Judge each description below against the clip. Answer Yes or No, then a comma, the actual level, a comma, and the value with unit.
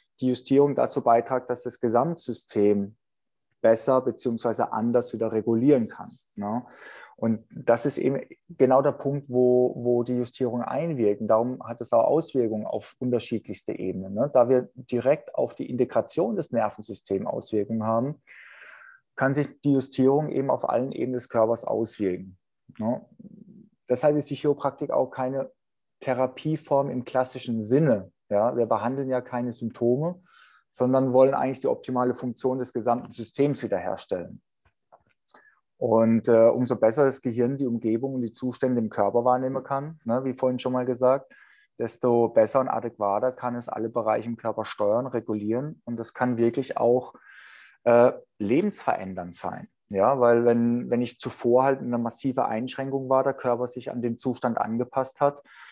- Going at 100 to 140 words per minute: No, average, 155 wpm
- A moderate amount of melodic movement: No, narrow, 2.3 semitones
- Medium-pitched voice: No, low, 125 Hz